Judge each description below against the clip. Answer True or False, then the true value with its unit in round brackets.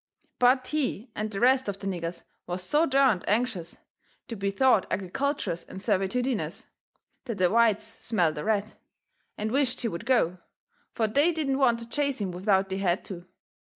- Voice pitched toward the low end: False (220 Hz)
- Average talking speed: True (175 wpm)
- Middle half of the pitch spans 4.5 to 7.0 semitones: True (5.2 semitones)